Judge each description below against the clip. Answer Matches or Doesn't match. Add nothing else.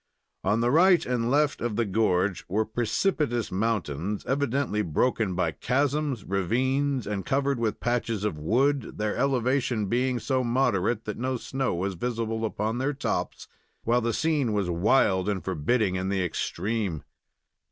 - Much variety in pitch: Doesn't match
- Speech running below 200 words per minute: Matches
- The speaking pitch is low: Matches